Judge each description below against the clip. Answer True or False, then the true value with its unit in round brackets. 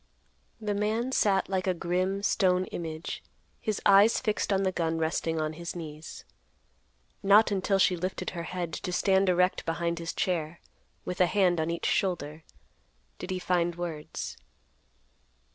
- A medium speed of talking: True (155 wpm)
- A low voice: False (180 Hz)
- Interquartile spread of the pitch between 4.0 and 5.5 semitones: False (2.6 semitones)